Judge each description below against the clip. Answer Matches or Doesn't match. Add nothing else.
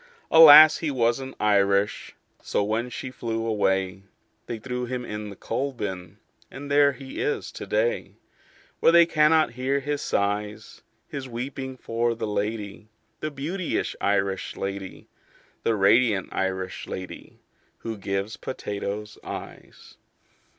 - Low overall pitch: Matches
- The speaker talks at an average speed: Doesn't match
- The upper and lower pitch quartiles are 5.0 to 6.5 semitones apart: Matches